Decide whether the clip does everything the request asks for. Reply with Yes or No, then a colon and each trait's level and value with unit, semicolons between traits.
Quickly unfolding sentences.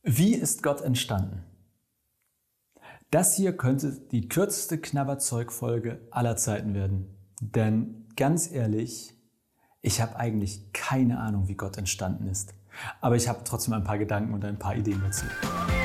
No: average, 140 wpm